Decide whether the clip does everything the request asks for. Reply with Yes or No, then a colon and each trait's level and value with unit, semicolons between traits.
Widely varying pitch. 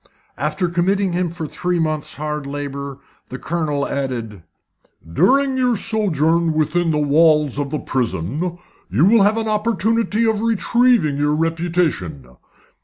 Yes: wide, 5.8 semitones